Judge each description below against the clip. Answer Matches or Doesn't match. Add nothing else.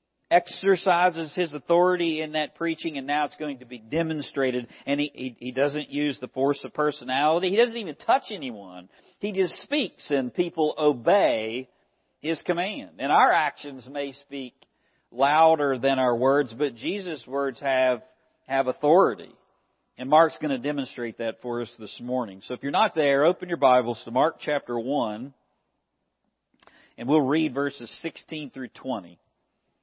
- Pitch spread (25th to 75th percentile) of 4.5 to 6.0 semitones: Doesn't match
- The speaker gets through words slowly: Doesn't match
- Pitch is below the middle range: Doesn't match